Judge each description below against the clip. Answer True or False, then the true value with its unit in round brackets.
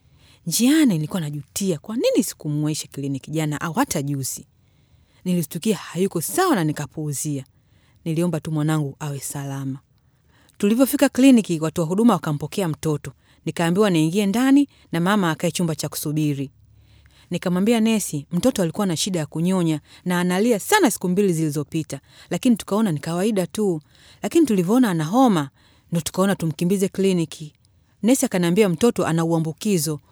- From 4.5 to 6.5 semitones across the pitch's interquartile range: True (5.2 semitones)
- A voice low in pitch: False (170 Hz)